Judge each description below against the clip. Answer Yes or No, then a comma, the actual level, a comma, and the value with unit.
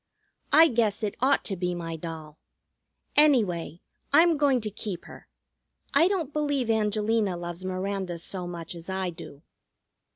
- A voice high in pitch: Yes, high, 200 Hz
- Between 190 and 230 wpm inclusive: No, average, 150 wpm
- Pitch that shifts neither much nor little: No, wide, 6.6 semitones